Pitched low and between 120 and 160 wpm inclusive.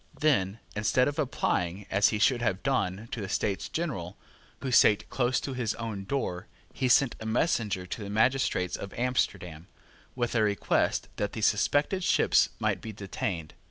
No: low, 110 Hz; average, 170 wpm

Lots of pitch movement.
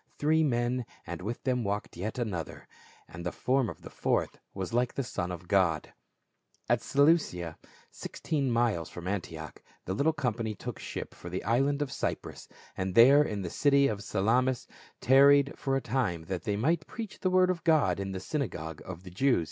Yes: wide, 7.0 semitones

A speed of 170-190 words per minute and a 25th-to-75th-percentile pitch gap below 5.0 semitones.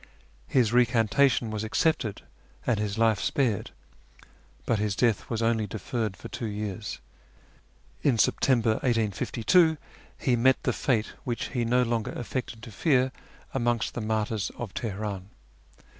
No: slow, 135 wpm; narrow, 2.6 semitones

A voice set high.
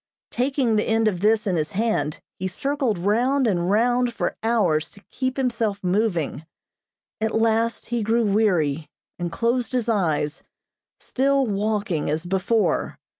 Yes: high, 220 Hz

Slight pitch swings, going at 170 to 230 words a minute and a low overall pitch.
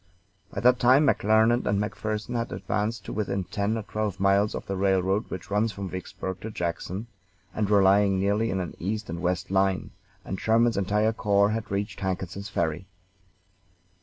Yes: narrow, 2.3 semitones; average, 175 wpm; low, 100 Hz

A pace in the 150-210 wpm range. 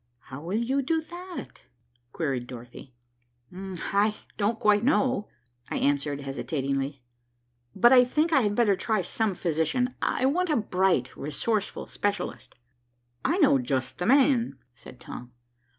No: slow, 135 wpm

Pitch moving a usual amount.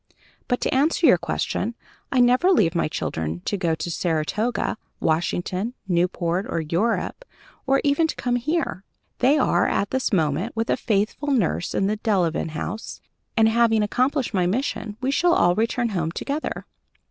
No: wide, 6.3 semitones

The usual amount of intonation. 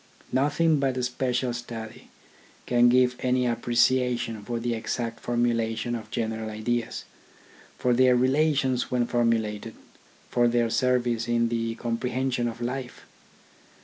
No: narrow, 1.5 semitones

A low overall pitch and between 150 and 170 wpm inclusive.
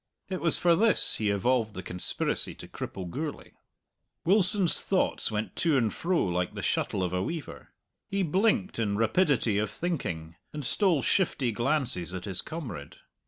Yes: low, 130 Hz; average, 165 wpm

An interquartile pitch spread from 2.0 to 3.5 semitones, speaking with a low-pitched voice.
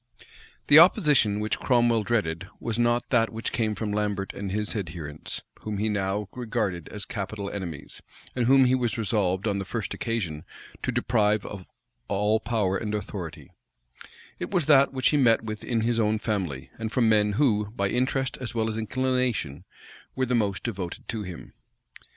Yes: average, 3.2 semitones; low, 110 Hz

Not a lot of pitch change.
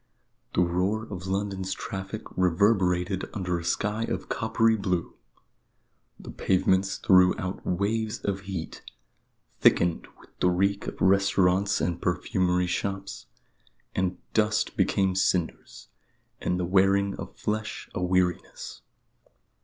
Yes: narrow, 1.8 semitones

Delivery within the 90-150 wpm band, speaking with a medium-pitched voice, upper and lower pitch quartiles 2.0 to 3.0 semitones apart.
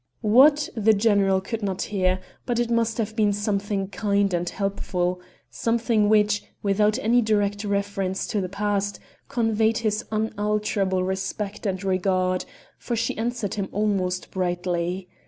No: average, 140 wpm; high, 205 Hz; narrow, 2.4 semitones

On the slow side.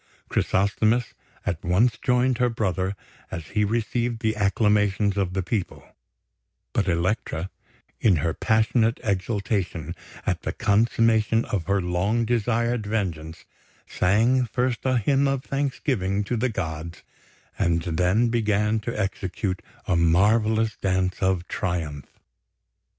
Yes: slow, 125 wpm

